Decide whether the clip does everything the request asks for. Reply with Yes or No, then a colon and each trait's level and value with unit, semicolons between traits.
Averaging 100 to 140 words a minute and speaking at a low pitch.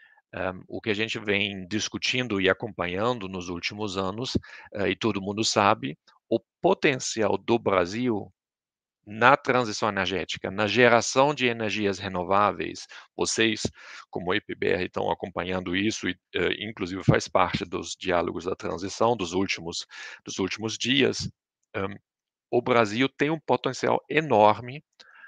Yes: average, 135 wpm; low, 110 Hz